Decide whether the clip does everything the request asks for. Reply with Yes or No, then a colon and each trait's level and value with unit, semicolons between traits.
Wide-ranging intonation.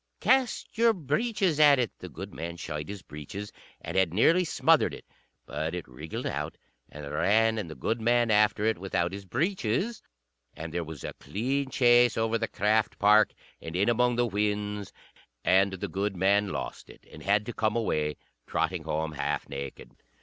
Yes: wide, 5.7 semitones